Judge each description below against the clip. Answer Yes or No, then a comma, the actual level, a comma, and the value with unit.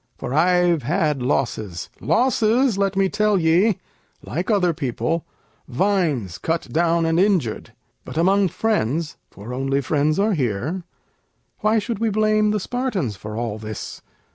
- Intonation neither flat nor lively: No, wide, 6.9 semitones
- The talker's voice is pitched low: No, medium, 170 Hz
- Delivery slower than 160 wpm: Yes, average, 140 wpm